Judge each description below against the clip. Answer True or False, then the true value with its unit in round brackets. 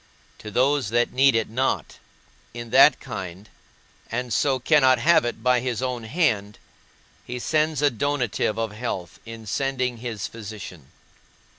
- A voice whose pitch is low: True (120 Hz)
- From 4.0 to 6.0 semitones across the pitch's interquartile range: False (3.3 semitones)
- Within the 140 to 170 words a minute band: True (145 wpm)